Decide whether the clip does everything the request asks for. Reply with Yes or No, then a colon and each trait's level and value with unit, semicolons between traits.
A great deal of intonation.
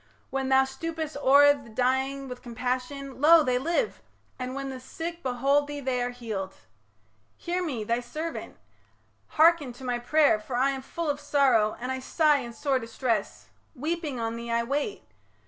No: average, 3.0 semitones